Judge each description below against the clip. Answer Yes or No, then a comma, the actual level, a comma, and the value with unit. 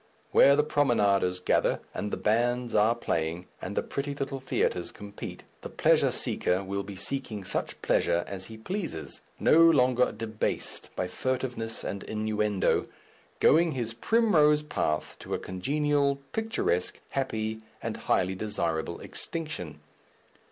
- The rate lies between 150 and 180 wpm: No, slow, 135 wpm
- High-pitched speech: No, low, 115 Hz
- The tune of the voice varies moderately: No, wide, 6.2 semitones